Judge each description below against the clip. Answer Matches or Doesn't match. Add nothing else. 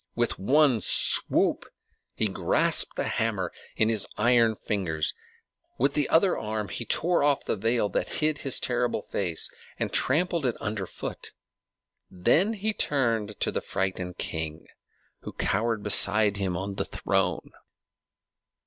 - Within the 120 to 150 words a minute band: Matches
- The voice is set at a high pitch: Doesn't match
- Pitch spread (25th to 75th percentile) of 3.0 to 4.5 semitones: Doesn't match